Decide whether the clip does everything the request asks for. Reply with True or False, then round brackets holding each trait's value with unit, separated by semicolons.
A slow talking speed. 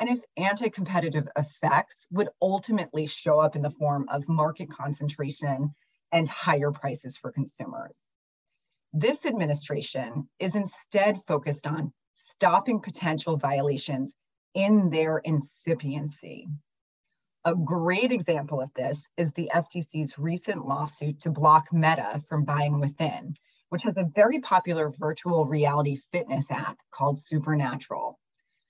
True (125 wpm)